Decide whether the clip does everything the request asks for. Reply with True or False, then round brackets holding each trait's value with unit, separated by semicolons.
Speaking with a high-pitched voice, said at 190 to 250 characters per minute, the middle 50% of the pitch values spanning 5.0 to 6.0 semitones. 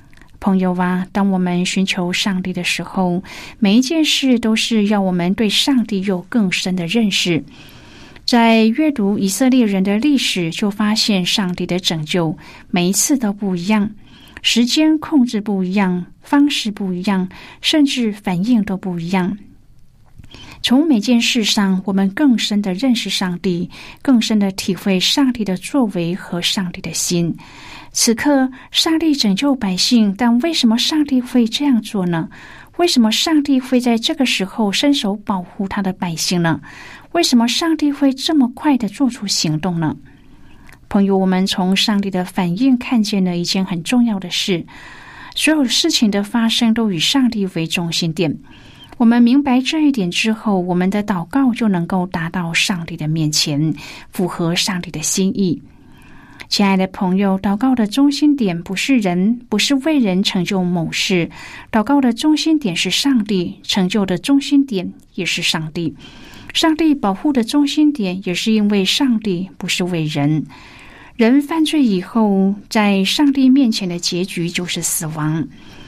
True (200 Hz; 240 characters per minute; 5.3 semitones)